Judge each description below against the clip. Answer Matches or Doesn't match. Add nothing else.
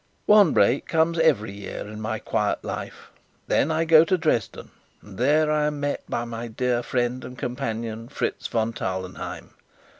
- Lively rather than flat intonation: Matches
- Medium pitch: Doesn't match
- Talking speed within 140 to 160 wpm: Doesn't match